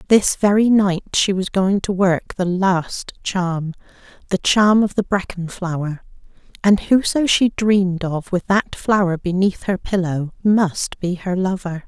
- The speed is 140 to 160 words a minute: Yes, average, 150 wpm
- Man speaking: No, female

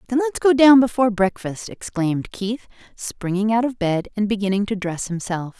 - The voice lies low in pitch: No, high, 215 Hz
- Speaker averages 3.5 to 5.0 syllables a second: No, 5.2 syllables/s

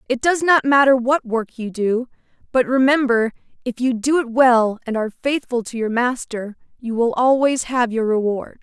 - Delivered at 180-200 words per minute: Yes, average, 190 wpm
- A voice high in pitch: Yes, high, 245 Hz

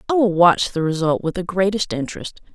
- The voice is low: No, medium, 185 Hz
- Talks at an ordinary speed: No, fast, 210 wpm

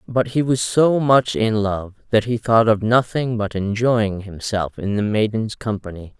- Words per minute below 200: Yes, average, 185 wpm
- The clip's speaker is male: Yes, male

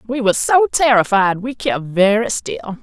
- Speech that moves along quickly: No, average, 170 wpm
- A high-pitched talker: Yes, high, 220 Hz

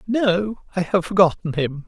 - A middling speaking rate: Yes, average, 160 wpm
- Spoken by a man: Yes, male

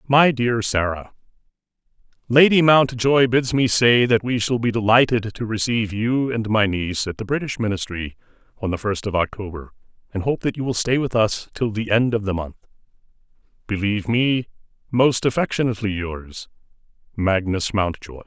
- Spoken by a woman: No, male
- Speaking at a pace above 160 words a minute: No, average, 155 wpm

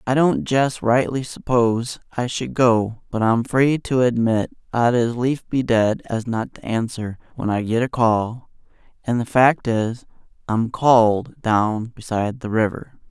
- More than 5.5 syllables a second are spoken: No, 4.0 syllables/s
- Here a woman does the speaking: No, male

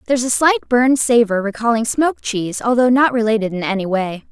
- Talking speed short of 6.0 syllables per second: No, 6.3 syllables/s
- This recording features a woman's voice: Yes, female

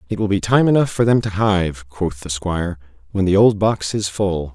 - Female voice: No, male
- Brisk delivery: Yes, fast, 240 wpm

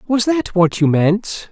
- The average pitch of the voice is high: Yes, high, 205 Hz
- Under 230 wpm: Yes, average, 200 wpm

